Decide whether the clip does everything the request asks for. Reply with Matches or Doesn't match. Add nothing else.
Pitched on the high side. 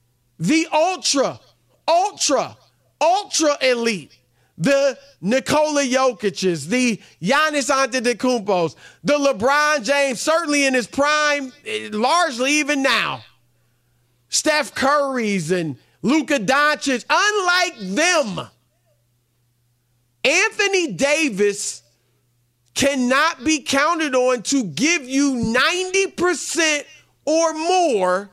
Matches